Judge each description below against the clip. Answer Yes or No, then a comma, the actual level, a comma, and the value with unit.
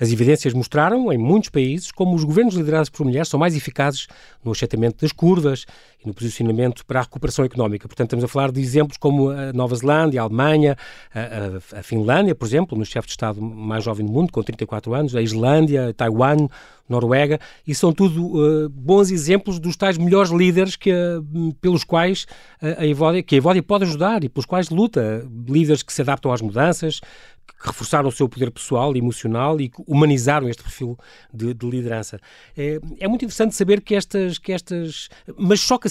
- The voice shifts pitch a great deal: Yes, wide, 5.9 semitones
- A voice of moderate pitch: Yes, medium, 145 Hz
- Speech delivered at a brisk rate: Yes, fast, 190 wpm